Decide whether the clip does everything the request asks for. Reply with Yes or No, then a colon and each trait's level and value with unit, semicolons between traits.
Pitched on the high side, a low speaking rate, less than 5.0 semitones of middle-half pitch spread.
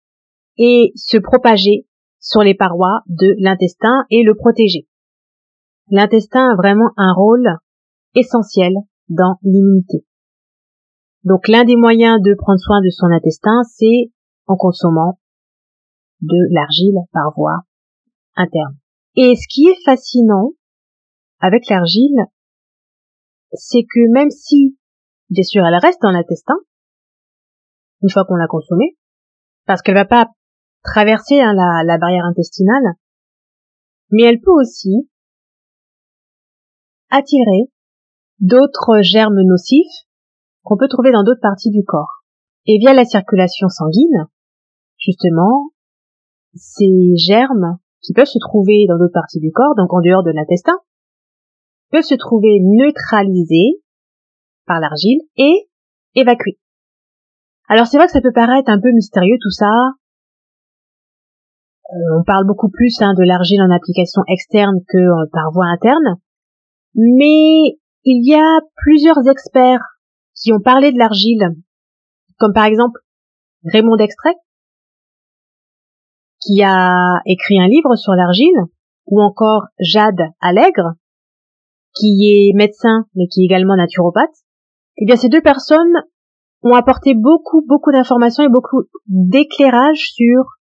No: high, 215 Hz; slow, 125 wpm; wide, 5.5 semitones